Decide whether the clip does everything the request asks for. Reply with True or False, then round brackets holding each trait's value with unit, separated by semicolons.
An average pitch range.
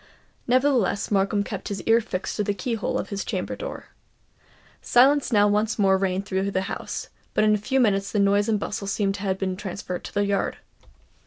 False (1.9 semitones)